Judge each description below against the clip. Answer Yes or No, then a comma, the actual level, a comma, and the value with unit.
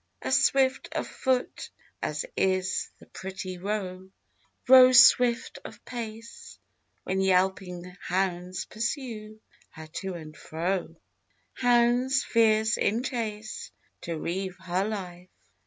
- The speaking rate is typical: No, slow, 110 wpm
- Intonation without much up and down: No, average, 4.4 semitones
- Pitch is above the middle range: Yes, high, 195 Hz